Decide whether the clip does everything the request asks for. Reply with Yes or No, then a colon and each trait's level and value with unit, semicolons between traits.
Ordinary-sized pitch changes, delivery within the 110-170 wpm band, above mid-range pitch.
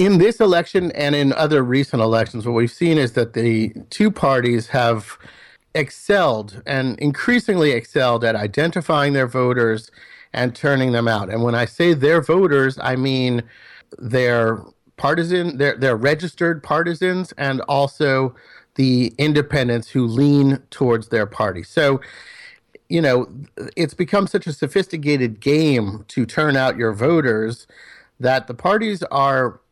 No: average, 4.7 semitones; average, 140 wpm; low, 135 Hz